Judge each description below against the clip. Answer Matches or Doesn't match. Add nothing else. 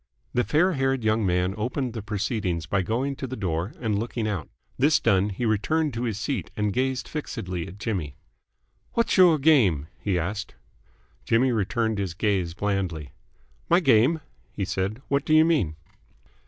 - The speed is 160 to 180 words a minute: Matches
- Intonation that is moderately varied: Doesn't match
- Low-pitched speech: Matches